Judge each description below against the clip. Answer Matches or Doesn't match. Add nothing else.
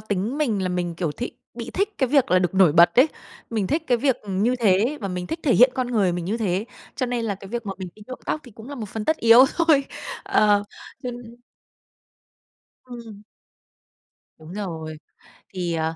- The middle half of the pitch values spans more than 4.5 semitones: Matches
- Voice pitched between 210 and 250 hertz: Matches